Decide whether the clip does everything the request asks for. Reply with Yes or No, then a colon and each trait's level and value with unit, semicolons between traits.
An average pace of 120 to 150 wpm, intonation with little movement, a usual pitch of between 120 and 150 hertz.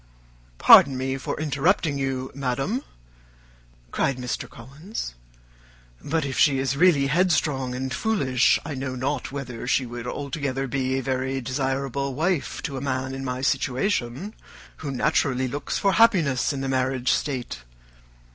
Yes: average, 145 wpm; narrow, 2.0 semitones; low, 135 Hz